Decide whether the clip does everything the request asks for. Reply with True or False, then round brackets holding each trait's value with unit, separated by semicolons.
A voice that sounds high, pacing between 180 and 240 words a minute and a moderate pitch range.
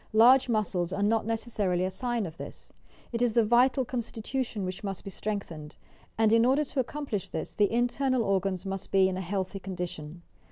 True (210 Hz; 190 wpm; 4.1 semitones)